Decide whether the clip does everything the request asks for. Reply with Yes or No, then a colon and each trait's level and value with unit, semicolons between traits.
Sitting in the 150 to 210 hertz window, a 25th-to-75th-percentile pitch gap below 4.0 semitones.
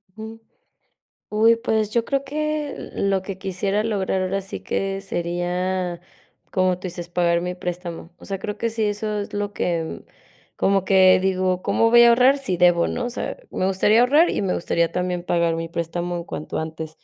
Yes: high, 190 Hz; average, 3.6 semitones